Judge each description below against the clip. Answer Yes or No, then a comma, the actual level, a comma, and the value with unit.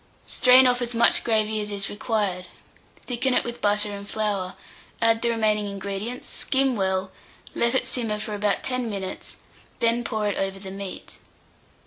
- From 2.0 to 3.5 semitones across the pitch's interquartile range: Yes, average, 2.9 semitones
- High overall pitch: Yes, high, 215 Hz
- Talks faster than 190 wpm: No, average, 165 wpm